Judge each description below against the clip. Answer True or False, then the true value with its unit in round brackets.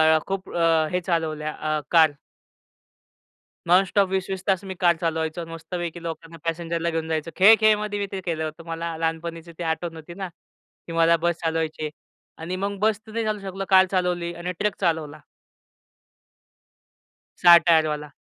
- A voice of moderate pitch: True (170 Hz)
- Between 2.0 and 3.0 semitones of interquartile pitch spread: True (2.6 semitones)